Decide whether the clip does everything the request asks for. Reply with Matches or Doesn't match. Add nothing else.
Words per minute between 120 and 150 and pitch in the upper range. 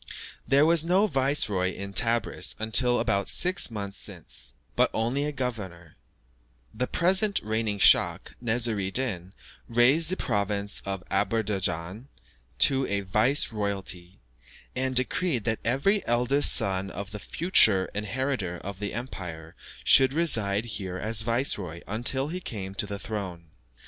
Doesn't match